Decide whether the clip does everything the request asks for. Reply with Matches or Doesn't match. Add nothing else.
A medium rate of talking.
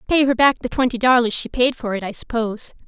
Doesn't match